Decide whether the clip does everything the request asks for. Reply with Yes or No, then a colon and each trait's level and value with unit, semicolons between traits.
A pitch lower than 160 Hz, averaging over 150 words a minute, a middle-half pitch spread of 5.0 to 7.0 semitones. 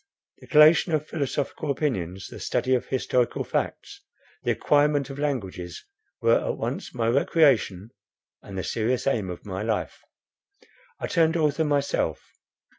No: low, 135 Hz; average, 140 wpm; wide, 5.6 semitones